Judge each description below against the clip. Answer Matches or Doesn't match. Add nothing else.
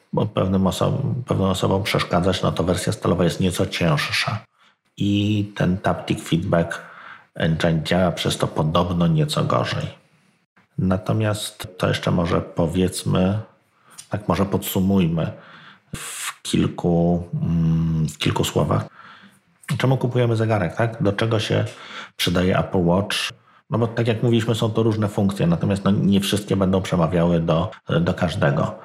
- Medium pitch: Doesn't match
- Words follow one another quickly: Doesn't match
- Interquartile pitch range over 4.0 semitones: Matches